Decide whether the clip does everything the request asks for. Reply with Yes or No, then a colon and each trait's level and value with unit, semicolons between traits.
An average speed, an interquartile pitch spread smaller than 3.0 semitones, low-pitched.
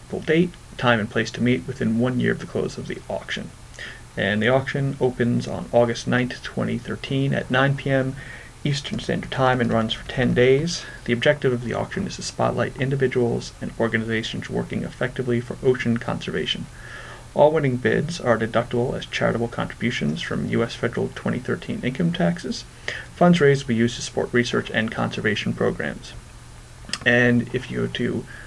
Yes: average, 165 wpm; narrow, 2.5 semitones; low, 125 Hz